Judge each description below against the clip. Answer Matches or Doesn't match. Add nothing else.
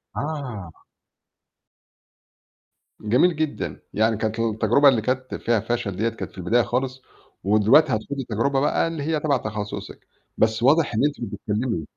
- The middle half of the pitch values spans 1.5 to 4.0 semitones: Doesn't match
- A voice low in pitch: Matches